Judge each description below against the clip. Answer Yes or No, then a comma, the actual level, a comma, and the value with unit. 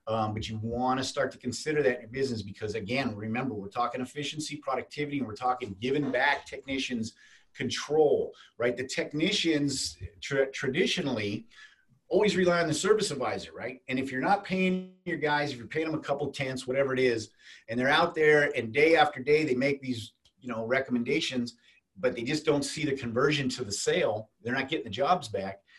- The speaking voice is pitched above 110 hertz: Yes, low, 135 Hz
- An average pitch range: Yes, average, 3.9 semitones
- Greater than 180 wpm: Yes, average, 200 wpm